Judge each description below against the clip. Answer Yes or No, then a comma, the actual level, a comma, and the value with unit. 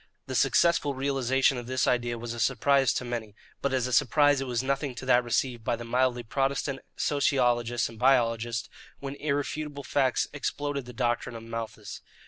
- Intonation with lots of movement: No, narrow, 2.6 semitones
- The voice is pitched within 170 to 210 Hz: No, low, 130 Hz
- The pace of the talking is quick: No, average, 175 wpm